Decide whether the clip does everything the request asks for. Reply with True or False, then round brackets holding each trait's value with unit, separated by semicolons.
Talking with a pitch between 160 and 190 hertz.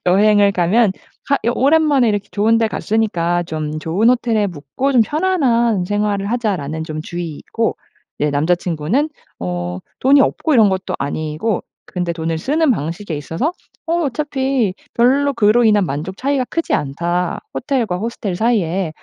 False (205 Hz)